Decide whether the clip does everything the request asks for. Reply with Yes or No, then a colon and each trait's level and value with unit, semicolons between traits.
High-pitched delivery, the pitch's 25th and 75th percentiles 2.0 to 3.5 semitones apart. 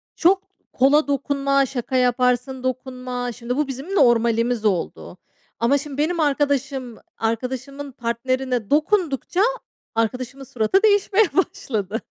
Yes: very high, 260 Hz; average, 2.9 semitones